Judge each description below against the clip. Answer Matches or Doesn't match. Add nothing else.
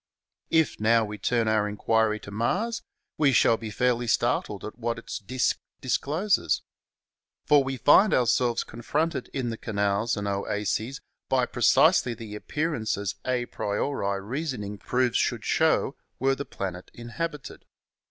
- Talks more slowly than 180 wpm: Matches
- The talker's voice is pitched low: Matches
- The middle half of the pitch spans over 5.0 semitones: Doesn't match